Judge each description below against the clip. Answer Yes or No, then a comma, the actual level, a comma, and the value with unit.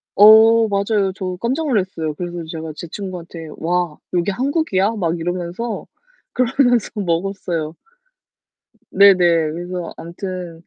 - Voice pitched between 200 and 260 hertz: No, medium, 185 Hz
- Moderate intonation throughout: Yes, average, 3.8 semitones